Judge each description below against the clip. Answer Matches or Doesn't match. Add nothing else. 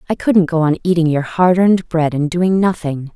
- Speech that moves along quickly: Matches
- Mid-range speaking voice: Matches